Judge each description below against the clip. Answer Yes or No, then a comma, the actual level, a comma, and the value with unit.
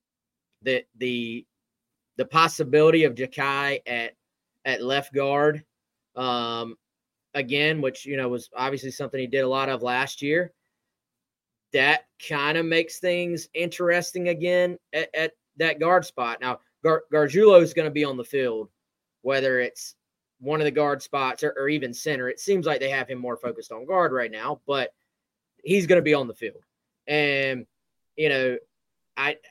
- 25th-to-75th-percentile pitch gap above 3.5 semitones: Yes, average, 3.9 semitones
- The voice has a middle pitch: Yes, medium, 145 Hz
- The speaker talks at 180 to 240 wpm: No, average, 165 wpm